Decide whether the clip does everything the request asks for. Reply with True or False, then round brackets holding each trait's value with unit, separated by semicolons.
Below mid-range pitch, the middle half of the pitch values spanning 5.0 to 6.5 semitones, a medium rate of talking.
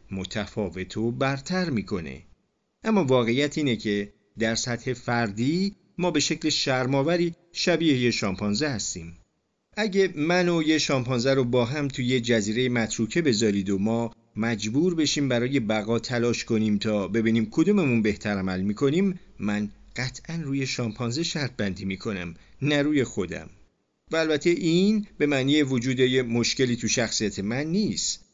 True (125 Hz; 5.5 semitones; 140 wpm)